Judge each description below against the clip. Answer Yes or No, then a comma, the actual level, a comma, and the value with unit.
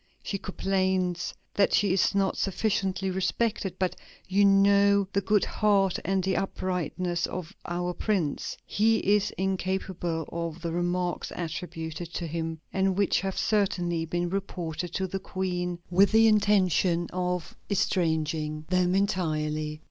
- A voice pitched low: No, medium, 185 Hz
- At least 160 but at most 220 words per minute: No, slow, 135 wpm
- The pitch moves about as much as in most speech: No, narrow, 2.2 semitones